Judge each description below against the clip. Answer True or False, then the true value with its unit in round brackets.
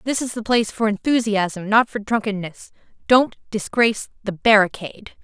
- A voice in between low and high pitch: False (215 Hz)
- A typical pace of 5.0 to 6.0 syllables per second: True (5.1 syllables/s)